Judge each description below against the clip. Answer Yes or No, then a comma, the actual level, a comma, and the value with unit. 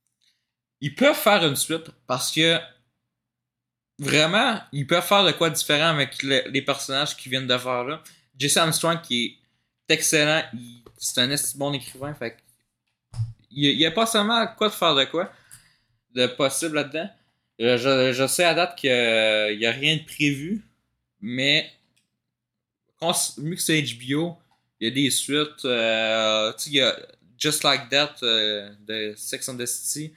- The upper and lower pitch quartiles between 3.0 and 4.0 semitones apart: No, average, 4.8 semitones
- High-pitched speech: No, medium, 140 Hz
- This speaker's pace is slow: No, average, 165 wpm